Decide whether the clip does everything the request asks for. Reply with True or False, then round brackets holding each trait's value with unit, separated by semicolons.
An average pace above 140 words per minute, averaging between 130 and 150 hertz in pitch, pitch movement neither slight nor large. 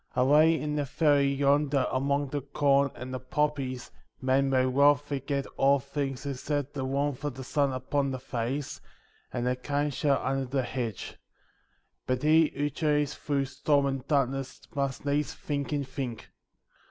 False (165 wpm; 140 Hz; 1.7 semitones)